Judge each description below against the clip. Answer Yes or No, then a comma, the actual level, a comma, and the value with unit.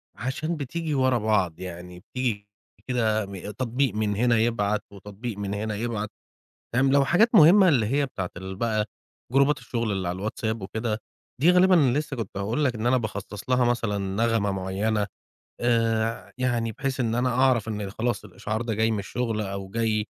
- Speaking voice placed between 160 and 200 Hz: No, low, 115 Hz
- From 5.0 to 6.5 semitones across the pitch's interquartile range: No, average, 3.7 semitones